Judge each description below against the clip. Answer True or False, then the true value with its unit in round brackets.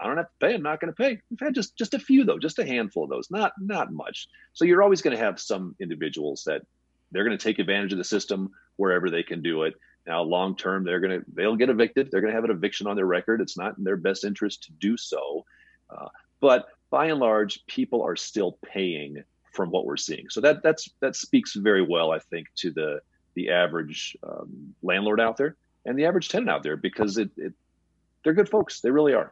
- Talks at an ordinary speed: False (245 wpm)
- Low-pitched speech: True (115 Hz)